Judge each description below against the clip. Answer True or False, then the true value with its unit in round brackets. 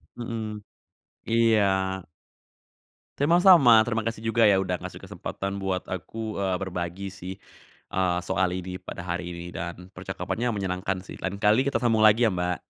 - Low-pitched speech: True (100 Hz)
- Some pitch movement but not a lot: True (3.6 semitones)